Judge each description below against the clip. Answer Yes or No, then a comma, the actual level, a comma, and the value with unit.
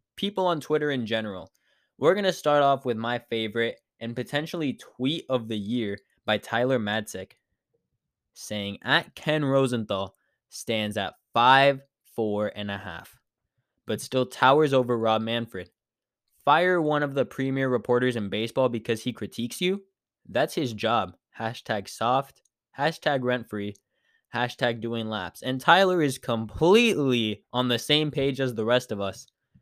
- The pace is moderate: Yes, average, 150 wpm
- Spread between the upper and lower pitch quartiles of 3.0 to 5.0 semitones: Yes, average, 3.9 semitones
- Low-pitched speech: Yes, low, 120 Hz